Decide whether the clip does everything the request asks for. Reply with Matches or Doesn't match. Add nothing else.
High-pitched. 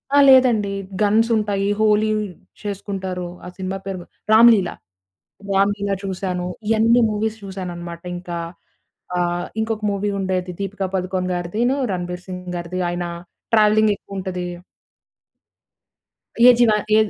Matches